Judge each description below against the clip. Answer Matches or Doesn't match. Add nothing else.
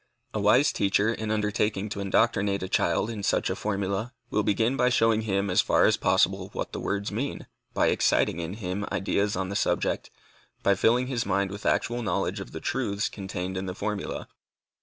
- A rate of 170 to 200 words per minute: Matches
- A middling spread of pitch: Doesn't match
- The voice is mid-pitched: Doesn't match